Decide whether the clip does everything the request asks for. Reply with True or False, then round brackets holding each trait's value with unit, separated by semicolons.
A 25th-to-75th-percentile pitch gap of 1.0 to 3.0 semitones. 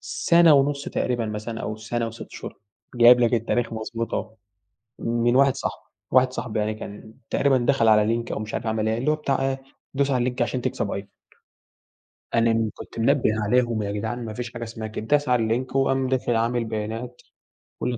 True (2.5 semitones)